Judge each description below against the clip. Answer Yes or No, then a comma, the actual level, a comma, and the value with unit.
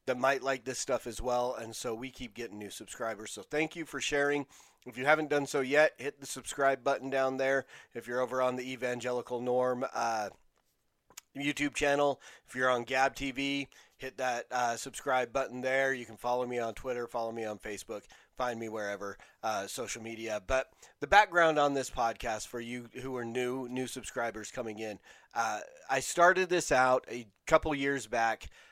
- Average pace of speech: Yes, average, 190 wpm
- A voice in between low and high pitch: No, low, 130 Hz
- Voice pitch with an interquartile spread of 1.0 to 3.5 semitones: Yes, narrow, 2.5 semitones